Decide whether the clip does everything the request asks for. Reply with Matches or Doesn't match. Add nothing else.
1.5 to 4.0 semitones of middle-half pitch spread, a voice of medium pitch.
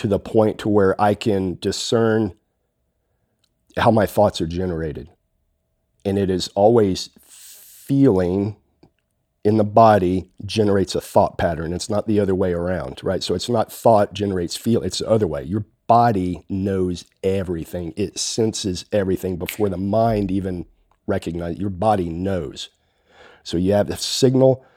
Doesn't match